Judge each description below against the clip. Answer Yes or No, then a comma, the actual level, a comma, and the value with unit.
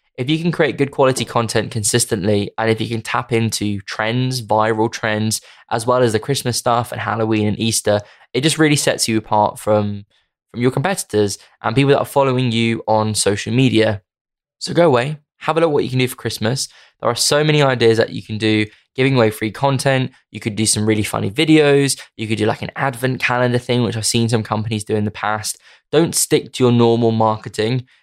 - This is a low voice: Yes, low, 115 Hz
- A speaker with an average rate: No, fast, 220 wpm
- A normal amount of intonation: Yes, average, 3.2 semitones